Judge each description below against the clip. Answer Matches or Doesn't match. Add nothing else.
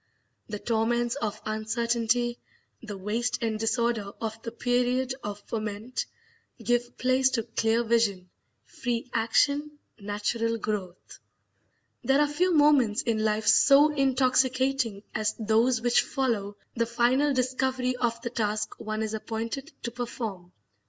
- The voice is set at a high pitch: Matches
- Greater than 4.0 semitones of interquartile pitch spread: Doesn't match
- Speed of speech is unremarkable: Doesn't match